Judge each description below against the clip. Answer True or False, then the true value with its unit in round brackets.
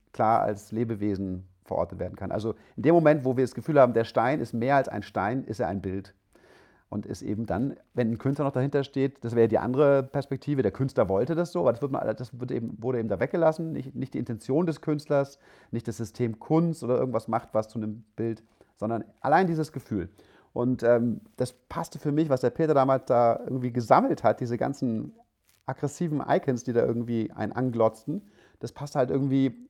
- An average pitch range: True (3.7 semitones)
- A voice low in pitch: True (125 Hz)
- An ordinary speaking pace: False (210 wpm)